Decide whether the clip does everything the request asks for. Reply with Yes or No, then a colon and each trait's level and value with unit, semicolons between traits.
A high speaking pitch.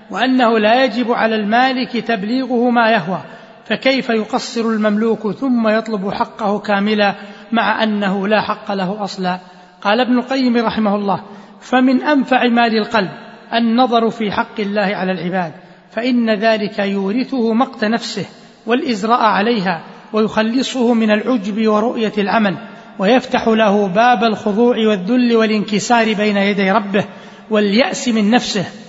Yes: high, 220 Hz